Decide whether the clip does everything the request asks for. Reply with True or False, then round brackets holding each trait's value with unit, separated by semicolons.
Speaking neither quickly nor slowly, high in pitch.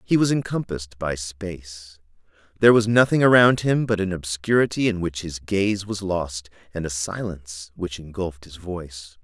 False (170 wpm; 95 Hz)